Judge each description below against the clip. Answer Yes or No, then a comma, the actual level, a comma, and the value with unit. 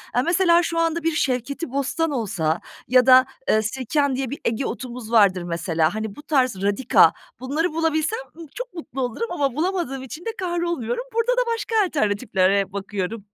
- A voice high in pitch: Yes, very high, 265 Hz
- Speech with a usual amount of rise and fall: No, wide, 7.2 semitones